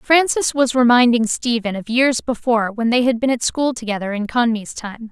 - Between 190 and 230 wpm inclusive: Yes, average, 200 wpm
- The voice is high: Yes, high, 240 Hz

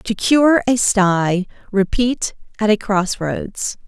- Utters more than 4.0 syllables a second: No, 3.1 syllables/s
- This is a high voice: Yes, high, 210 Hz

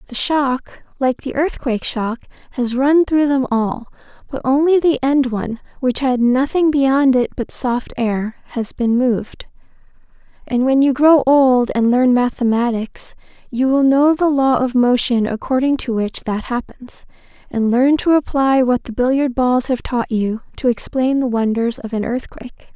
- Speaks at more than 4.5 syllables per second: No, 4.4 syllables/s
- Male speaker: No, female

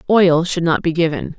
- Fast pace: Yes, fast, 215 wpm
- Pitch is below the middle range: No, medium, 165 Hz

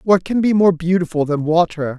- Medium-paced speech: No, fast, 210 wpm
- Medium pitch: Yes, medium, 170 Hz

